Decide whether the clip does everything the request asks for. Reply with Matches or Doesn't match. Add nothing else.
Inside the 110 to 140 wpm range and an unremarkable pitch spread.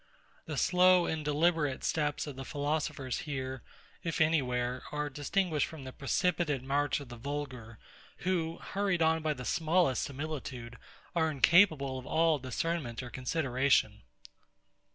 Matches